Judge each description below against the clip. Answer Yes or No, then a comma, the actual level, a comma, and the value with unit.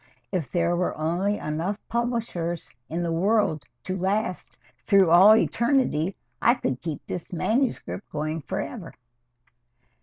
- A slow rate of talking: Yes, slow, 125 wpm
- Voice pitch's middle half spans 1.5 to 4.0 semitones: No, average, 4.7 semitones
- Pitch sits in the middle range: Yes, medium, 180 Hz